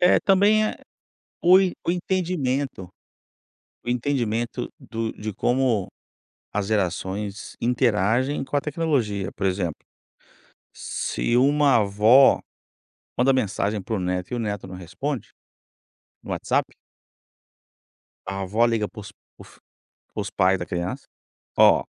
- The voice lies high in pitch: No, low, 115 Hz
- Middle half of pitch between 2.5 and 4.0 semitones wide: No, wide, 5.6 semitones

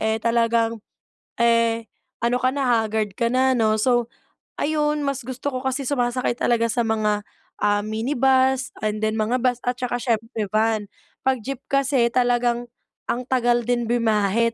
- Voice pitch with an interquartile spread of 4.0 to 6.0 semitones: No, narrow, 2.5 semitones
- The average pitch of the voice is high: Yes, high, 235 Hz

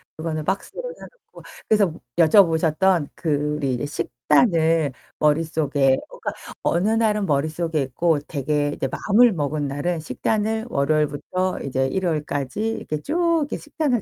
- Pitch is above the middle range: No, medium, 160 Hz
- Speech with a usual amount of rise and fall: No, wide, 5.7 semitones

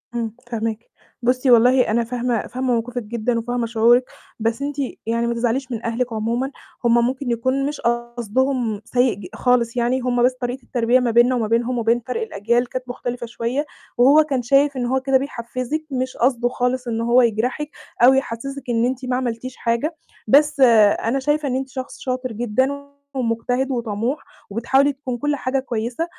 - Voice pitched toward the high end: Yes, high, 245 Hz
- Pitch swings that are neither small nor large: No, narrow, 2.0 semitones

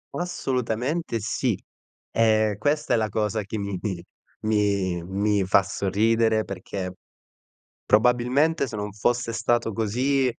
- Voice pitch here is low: Yes, low, 110 Hz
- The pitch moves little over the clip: No, average, 3.3 semitones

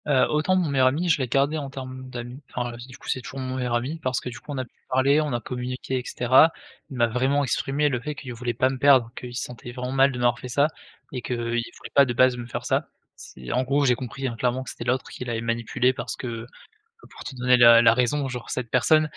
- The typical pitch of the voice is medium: No, low, 125 Hz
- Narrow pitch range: Yes, narrow, 2.0 semitones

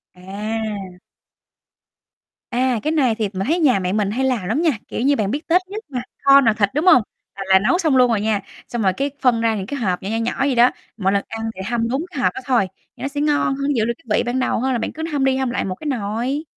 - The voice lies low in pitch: No, high, 240 Hz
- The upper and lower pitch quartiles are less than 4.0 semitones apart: No, average, 4.7 semitones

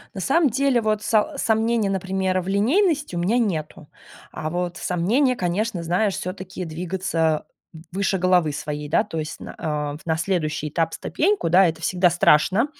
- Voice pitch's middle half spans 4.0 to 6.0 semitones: Yes, average, 4.8 semitones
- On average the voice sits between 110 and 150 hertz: No, medium, 185 Hz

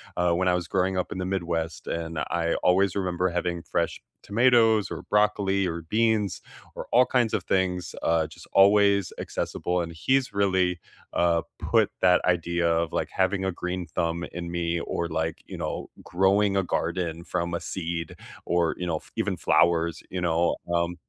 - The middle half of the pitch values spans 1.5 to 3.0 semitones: Yes, narrow, 2.4 semitones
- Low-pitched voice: Yes, very low, 90 Hz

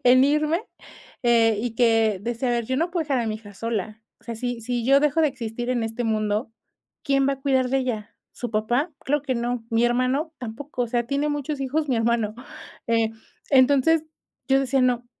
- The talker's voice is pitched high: Yes, high, 245 Hz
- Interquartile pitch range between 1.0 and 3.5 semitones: Yes, average, 3.2 semitones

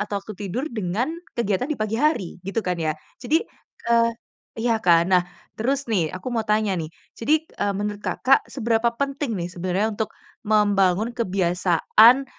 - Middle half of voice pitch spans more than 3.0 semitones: Yes, average, 4.2 semitones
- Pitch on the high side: Yes, high, 215 Hz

